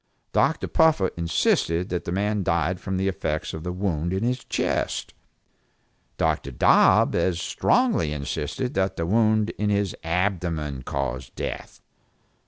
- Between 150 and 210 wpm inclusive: No, average, 140 wpm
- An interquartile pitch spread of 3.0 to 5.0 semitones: Yes, average, 3.9 semitones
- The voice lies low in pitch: Yes, very low, 90 Hz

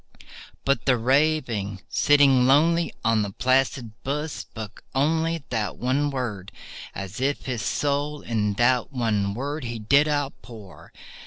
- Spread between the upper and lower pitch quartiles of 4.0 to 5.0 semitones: Yes, average, 4.5 semitones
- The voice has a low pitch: Yes, low, 130 Hz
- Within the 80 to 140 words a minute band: Yes, slow, 135 wpm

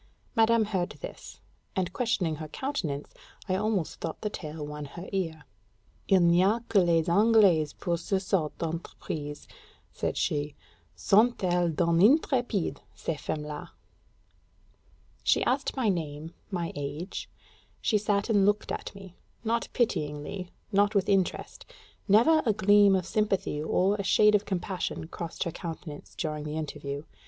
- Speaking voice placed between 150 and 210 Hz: Yes, medium, 185 Hz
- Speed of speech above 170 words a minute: No, average, 145 wpm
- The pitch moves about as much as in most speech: Yes, average, 4.7 semitones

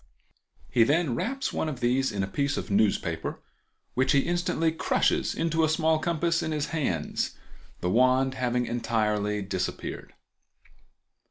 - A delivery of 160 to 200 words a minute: No, average, 145 wpm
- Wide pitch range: Yes, wide, 6.0 semitones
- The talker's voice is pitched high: No, low, 130 Hz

